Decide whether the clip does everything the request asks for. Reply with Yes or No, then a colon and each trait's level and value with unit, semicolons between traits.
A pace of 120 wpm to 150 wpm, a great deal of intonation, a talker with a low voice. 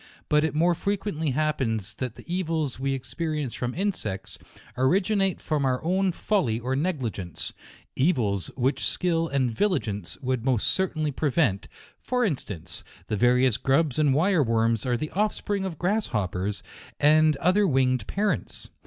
No: average, 145 wpm; wide, 6.4 semitones; medium, 145 Hz